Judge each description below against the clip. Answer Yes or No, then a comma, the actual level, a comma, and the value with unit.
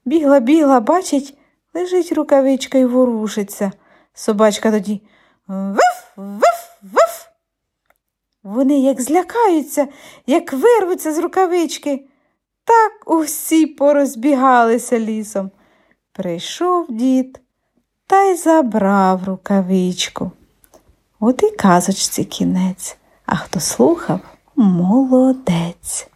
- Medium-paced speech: No, slow, 80 wpm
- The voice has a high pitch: Yes, very high, 270 Hz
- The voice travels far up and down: Yes, wide, 7.0 semitones